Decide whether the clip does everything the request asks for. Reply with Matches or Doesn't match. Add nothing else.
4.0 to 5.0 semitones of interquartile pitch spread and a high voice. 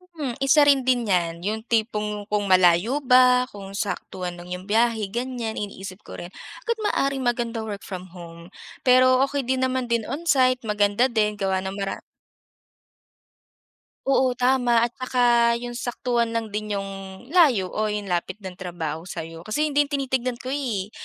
Matches